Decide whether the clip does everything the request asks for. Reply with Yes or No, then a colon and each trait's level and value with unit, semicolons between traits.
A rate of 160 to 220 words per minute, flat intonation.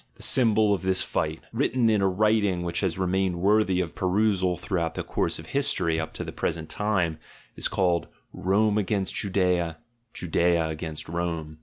No: average, 170 wpm; average, 3.5 semitones